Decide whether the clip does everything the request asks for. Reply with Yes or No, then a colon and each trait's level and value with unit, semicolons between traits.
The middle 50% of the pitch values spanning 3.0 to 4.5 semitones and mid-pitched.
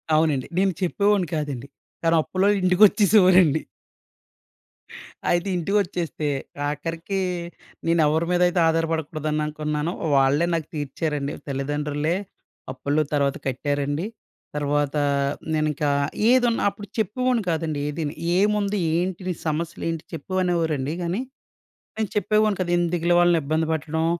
Yes: average, 3.7 semitones; medium, 165 Hz